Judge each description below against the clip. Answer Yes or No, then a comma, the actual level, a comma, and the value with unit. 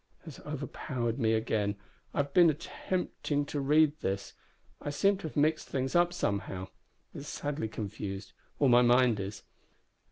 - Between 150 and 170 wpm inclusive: Yes, average, 155 wpm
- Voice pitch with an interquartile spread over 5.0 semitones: Yes, wide, 5.4 semitones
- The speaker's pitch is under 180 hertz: Yes, low, 135 Hz